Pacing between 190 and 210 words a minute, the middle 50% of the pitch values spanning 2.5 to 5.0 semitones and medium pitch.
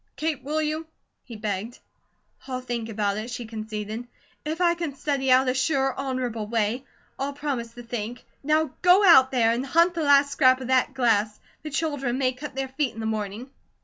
No: average, 195 wpm; average, 3.8 semitones; very high, 260 Hz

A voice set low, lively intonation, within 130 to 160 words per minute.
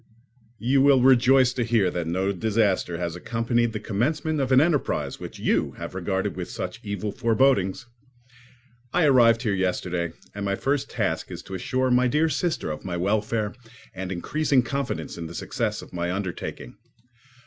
No: low, 115 Hz; wide, 5.7 semitones; average, 170 wpm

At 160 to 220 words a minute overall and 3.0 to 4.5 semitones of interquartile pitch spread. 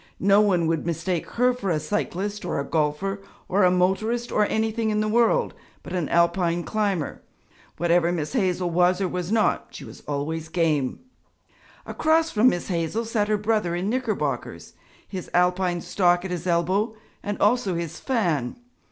Yes: average, 170 wpm; average, 3.8 semitones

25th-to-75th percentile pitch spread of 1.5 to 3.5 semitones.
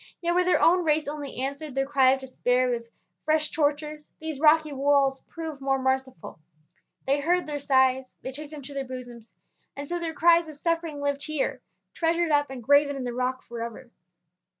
Yes: average, 2.9 semitones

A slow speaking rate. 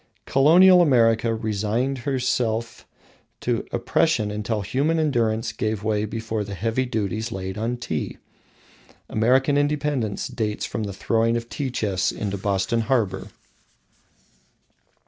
Yes: slow, 120 wpm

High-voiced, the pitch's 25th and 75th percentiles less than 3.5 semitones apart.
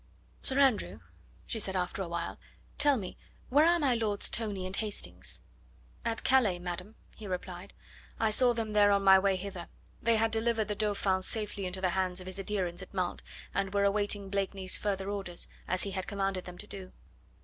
Yes: high, 200 Hz; narrow, 2.5 semitones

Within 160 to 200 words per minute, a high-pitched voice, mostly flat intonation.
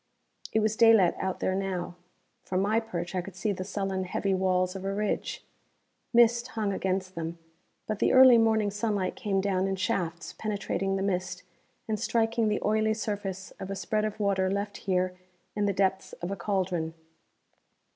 Yes: average, 175 wpm; high, 195 Hz; narrow, 2.3 semitones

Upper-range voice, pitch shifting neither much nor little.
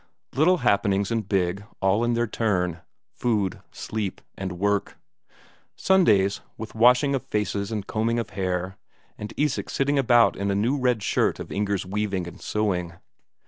No: low, 105 Hz; average, 3.5 semitones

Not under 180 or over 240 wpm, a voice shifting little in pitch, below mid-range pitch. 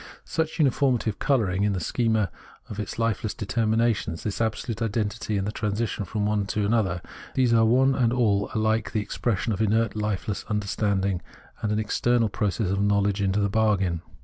Yes: average, 185 wpm; narrow, 2.2 semitones; low, 105 Hz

